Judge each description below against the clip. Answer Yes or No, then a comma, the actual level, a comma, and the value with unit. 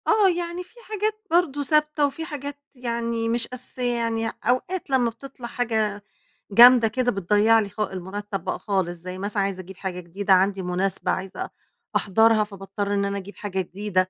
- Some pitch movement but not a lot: Yes, average, 4.4 semitones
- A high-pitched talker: Yes, high, 220 Hz